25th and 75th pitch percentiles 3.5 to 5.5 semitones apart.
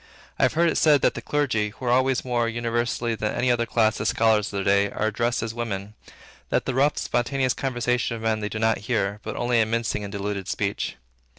No: narrow, 2.6 semitones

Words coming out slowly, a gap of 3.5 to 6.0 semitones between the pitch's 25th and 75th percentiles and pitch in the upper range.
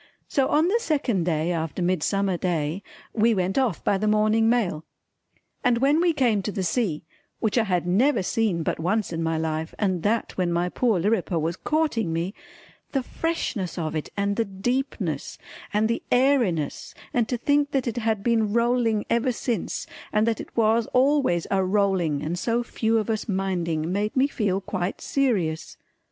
No: average, 180 wpm; average, 5.1 semitones; high, 210 Hz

